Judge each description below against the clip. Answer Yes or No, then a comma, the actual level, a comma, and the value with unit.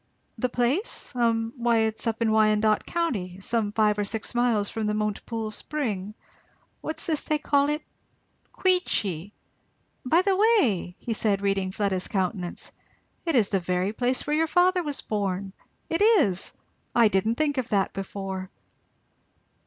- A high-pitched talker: Yes, high, 220 Hz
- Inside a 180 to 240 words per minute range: No, average, 155 wpm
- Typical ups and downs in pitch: No, wide, 6.3 semitones